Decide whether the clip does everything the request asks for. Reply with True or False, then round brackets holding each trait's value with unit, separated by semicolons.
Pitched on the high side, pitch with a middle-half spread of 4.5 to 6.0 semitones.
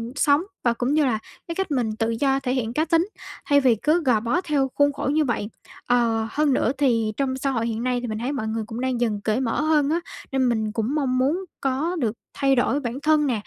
False (260 Hz; 3.9 semitones)